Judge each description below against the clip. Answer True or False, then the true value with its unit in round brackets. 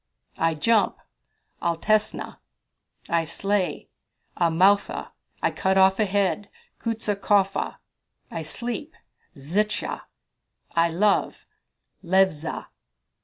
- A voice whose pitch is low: False (190 Hz)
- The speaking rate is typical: False (80 wpm)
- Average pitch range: True (3.6 semitones)